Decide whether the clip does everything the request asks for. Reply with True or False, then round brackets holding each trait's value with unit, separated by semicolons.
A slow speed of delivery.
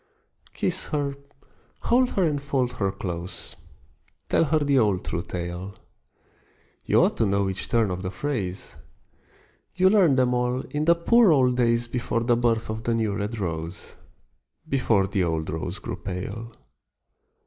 False (160 wpm)